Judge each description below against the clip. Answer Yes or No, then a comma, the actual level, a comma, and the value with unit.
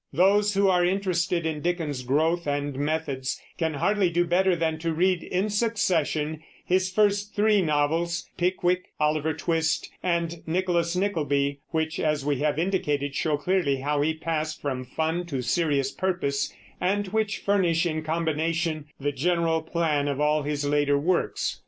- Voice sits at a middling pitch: Yes, medium, 160 Hz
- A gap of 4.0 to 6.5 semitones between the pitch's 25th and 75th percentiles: No, average, 3.4 semitones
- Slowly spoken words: No, average, 155 wpm